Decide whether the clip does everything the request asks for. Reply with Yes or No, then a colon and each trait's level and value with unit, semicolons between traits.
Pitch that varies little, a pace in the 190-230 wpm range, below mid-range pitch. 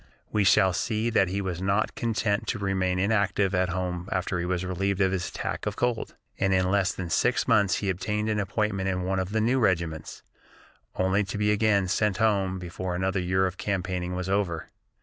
Yes: narrow, 1.9 semitones; fast, 205 wpm; very low, 95 Hz